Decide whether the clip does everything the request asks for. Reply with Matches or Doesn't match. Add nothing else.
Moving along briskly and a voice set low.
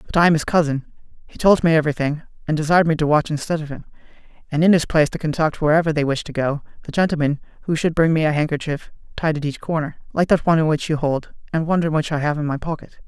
Doesn't match